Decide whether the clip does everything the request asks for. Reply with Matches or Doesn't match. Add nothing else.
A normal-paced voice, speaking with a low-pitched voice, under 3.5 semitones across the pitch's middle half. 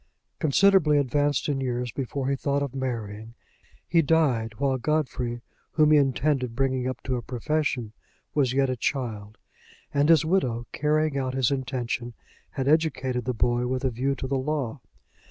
Matches